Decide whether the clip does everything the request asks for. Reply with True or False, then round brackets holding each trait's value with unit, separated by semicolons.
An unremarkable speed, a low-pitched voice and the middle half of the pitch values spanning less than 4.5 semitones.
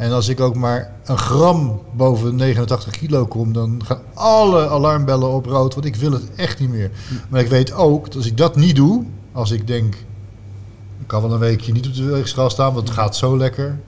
False (225 wpm; 125 Hz; 2.9 semitones)